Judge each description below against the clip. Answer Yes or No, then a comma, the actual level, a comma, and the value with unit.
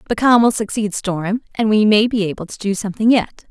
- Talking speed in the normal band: No, fast, 240 wpm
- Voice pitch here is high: Yes, high, 210 Hz